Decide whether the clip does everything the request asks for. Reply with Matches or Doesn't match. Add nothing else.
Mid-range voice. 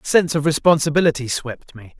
Matches